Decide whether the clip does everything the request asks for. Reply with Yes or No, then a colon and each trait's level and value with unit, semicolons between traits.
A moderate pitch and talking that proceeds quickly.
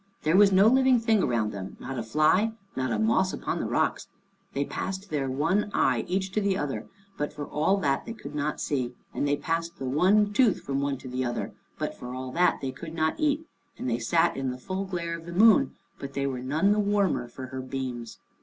Yes: medium, 155 Hz; fast, 230 wpm